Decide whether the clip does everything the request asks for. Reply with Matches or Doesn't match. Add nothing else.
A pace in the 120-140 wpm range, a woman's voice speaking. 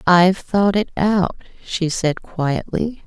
Matches